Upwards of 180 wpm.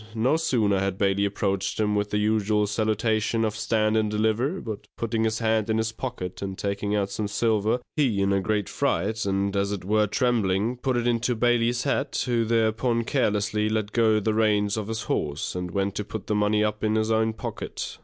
Yes: fast, 205 wpm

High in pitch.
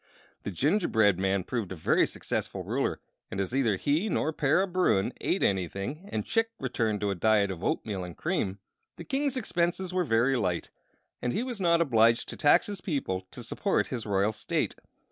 No: low, 120 Hz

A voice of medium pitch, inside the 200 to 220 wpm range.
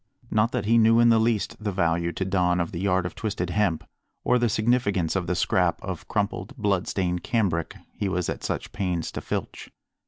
No: very low, 95 Hz; fast, 205 wpm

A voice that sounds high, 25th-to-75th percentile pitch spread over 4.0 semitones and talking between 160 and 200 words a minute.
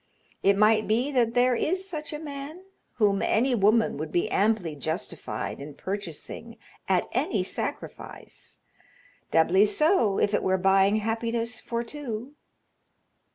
No: high, 220 Hz; average, 4.4 semitones; slow, 135 wpm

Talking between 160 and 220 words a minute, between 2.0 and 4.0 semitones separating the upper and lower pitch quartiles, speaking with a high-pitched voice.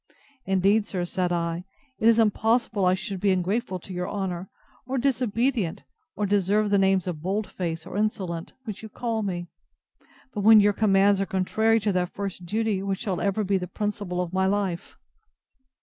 Yes: average, 180 wpm; average, 2.7 semitones; high, 195 Hz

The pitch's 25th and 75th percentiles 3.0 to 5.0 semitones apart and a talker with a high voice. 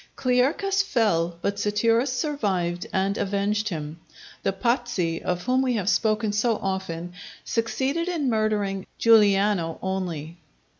Yes: average, 4.3 semitones; high, 210 Hz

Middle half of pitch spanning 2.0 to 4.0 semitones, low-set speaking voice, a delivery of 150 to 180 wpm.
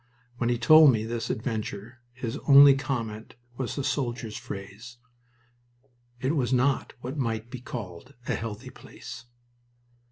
No: average, 2.8 semitones; low, 120 Hz; slow, 135 wpm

